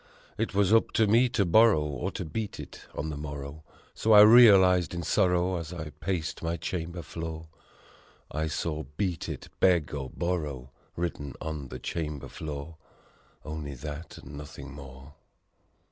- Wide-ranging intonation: No, average, 3.7 semitones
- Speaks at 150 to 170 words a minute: Yes, average, 160 wpm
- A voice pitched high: No, very low, 80 Hz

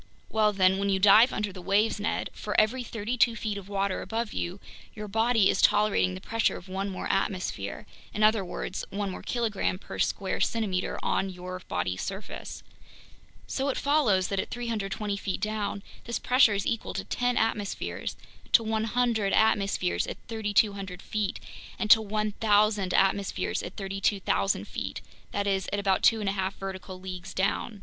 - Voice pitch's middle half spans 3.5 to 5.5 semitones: No, narrow, 2.4 semitones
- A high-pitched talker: Yes, high, 205 Hz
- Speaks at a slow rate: No, average, 175 wpm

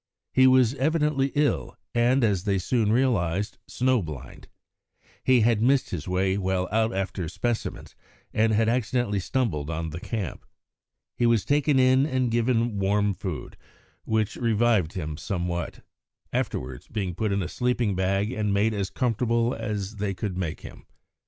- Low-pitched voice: Yes, low, 110 Hz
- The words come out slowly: No, average, 155 wpm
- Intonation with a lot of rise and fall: No, average, 4.4 semitones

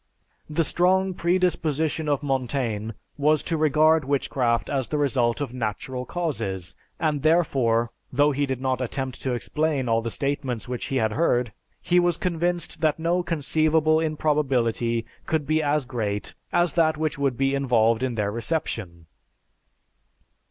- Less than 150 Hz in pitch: Yes, medium, 140 Hz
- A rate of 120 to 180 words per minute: Yes, average, 150 wpm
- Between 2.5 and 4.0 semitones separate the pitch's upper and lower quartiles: No, average, 4.6 semitones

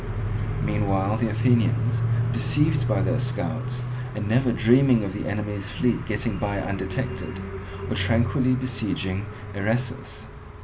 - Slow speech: Yes, slow, 120 wpm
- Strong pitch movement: No, average, 3.3 semitones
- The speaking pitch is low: Yes, low, 115 Hz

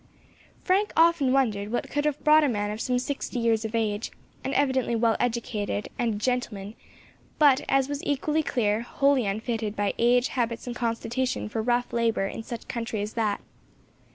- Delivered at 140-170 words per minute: No, average, 180 wpm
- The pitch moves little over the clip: No, average, 3.4 semitones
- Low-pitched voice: No, high, 235 Hz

